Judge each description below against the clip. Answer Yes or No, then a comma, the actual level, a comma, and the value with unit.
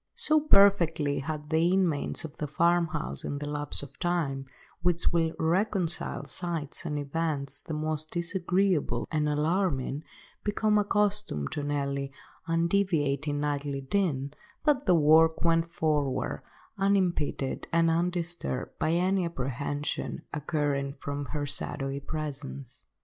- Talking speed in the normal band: No, slow, 120 wpm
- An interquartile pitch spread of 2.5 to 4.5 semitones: Yes, average, 3.5 semitones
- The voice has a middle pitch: Yes, medium, 155 Hz